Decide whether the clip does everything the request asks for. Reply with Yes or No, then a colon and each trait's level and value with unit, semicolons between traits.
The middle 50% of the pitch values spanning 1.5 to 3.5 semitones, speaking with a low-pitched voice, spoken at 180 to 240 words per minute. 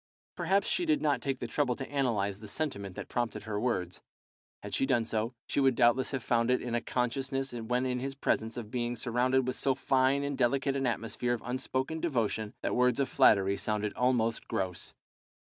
Yes: average, 2.8 semitones; low, 125 Hz; average, 200 wpm